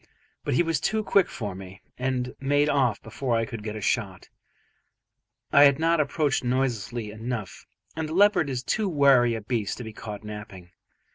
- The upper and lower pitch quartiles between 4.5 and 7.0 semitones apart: Yes, average, 5.0 semitones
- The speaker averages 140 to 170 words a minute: No, average, 185 wpm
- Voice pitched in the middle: No, low, 125 Hz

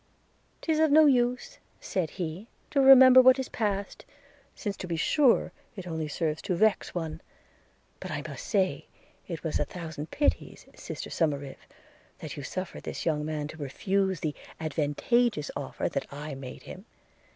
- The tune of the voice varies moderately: No, wide, 7.4 semitones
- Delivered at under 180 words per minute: Yes, average, 160 wpm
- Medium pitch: Yes, medium, 180 Hz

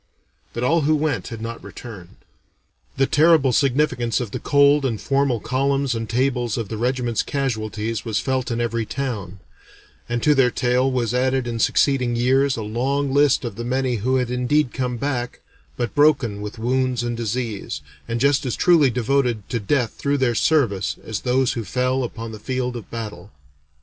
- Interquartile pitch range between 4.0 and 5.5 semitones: No, average, 2.9 semitones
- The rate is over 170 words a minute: Yes, average, 180 wpm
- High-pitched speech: No, low, 125 Hz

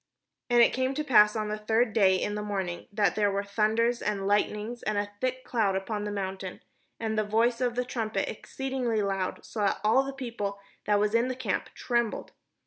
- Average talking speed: No, fast, 210 wpm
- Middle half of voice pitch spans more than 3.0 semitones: No, average, 2.7 semitones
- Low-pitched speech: No, high, 215 Hz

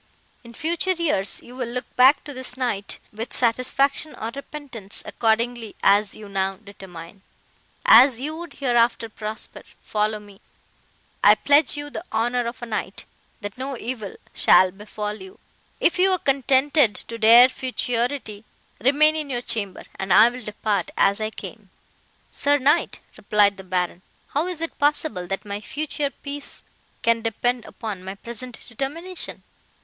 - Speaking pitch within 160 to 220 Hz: No, high, 235 Hz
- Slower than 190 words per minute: Yes, average, 150 wpm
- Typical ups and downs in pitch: Yes, average, 5.0 semitones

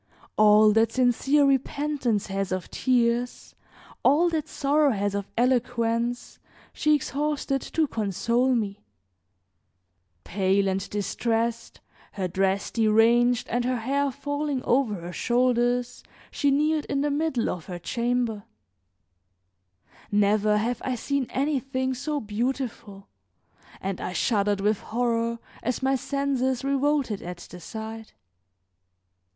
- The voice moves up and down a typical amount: Yes, average, 4.5 semitones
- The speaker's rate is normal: No, slow, 120 wpm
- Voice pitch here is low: No, high, 240 Hz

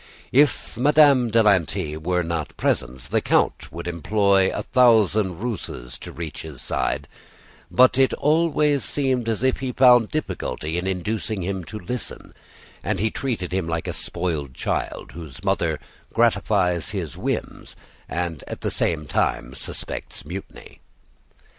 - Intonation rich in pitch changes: Yes, wide, 7.0 semitones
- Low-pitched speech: Yes, very low, 95 Hz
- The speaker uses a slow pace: No, average, 145 wpm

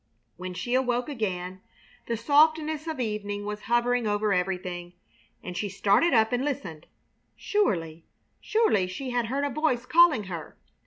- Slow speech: No, average, 150 wpm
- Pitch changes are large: Yes, wide, 6.8 semitones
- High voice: Yes, high, 225 Hz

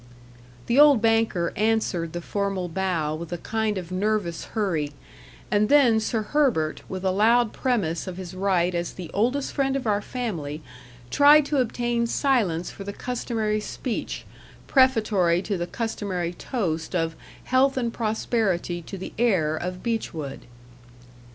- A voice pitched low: No, high, 205 Hz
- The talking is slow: No, average, 150 wpm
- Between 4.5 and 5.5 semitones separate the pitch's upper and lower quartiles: Yes, average, 5.2 semitones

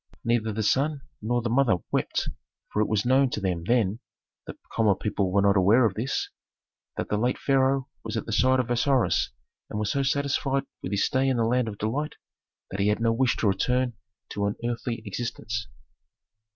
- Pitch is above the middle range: No, low, 115 Hz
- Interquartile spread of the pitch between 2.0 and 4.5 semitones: Yes, average, 3.7 semitones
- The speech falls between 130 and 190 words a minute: No, average, 200 wpm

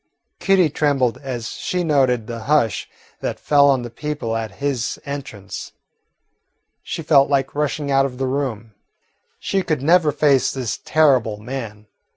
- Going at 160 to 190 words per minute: No, average, 150 wpm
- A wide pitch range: No, average, 3.9 semitones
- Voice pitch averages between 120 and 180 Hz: Yes, low, 135 Hz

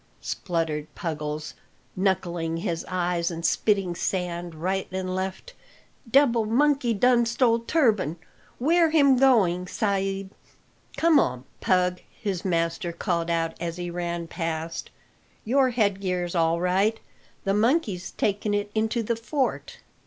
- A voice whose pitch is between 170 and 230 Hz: Yes, high, 190 Hz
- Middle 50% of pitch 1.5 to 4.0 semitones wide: No, average, 4.9 semitones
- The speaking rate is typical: No, slow, 125 wpm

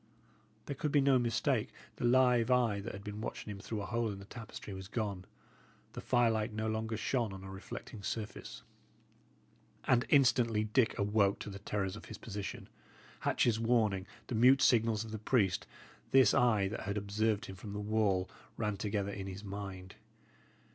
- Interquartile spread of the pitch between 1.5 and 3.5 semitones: Yes, average, 2.7 semitones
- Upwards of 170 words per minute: Yes, average, 180 wpm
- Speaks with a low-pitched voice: Yes, low, 110 Hz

